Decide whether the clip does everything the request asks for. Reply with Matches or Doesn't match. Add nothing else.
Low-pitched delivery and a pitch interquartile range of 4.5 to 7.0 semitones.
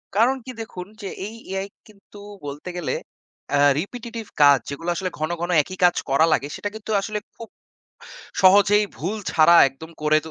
Doesn't match